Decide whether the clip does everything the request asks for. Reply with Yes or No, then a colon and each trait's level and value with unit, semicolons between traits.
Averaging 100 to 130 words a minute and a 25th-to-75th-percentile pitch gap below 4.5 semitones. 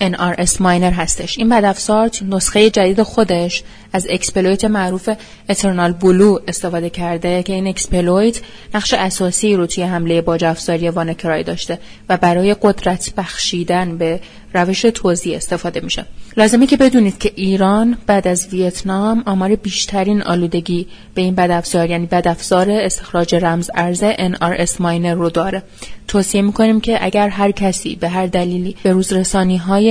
No: average, 140 wpm; narrow, 2.6 semitones